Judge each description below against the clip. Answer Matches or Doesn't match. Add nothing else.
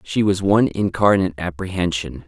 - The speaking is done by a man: Matches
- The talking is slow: Matches